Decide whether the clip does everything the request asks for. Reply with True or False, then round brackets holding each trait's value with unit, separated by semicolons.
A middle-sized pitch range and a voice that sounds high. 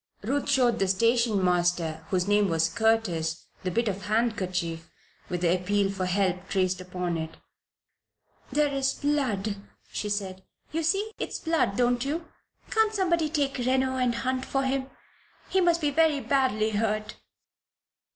False (6.6 semitones; 220 Hz)